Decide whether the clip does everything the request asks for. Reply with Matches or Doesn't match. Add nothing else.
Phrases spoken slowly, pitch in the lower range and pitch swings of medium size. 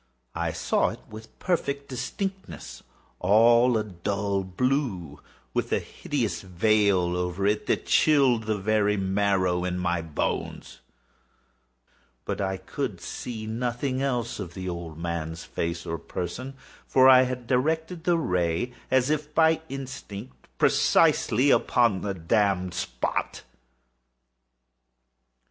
Doesn't match